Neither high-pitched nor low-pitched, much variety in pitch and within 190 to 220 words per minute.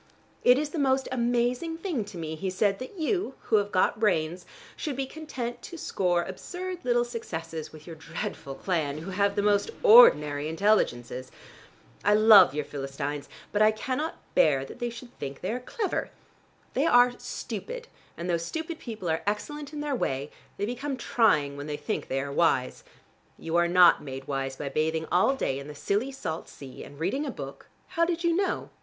No: high, 205 Hz; wide, 8.9 semitones; average, 195 wpm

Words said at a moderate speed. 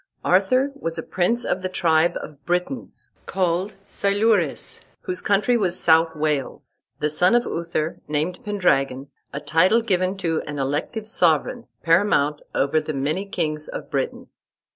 Yes: average, 145 wpm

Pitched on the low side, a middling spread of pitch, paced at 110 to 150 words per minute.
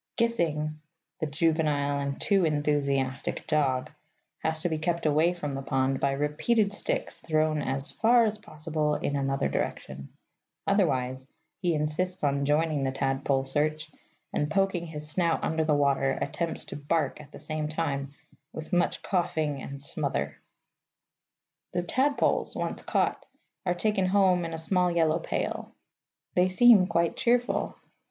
No: medium, 155 Hz; average, 3.9 semitones; average, 145 wpm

